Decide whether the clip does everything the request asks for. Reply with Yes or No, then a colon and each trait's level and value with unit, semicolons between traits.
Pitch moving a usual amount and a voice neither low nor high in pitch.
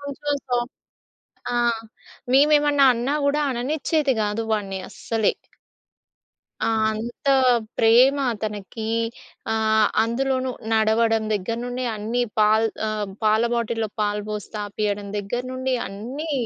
No: average, 3.4 semitones; high, 230 Hz